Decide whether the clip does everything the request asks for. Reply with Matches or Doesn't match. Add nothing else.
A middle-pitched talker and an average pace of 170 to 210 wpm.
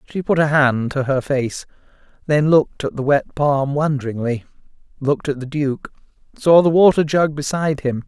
Matches